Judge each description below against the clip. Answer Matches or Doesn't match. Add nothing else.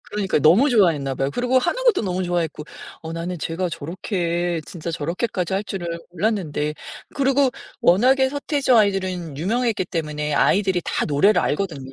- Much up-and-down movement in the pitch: Doesn't match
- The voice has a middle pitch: Matches